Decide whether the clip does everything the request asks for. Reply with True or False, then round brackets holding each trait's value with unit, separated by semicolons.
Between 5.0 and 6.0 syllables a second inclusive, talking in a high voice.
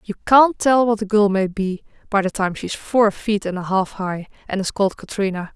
True (5.1 syllables/s; 205 Hz)